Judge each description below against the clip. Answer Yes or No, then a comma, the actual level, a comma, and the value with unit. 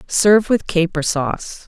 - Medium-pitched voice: Yes, medium, 180 Hz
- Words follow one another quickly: No, average, 145 wpm